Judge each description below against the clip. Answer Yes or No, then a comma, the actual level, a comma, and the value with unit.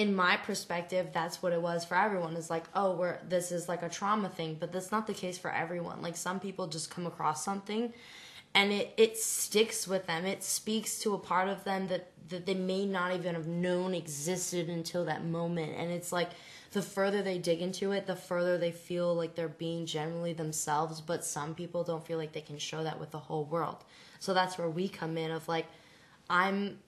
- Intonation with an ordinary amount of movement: No, narrow, 2.3 semitones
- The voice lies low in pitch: No, medium, 175 Hz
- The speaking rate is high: Yes, fast, 220 wpm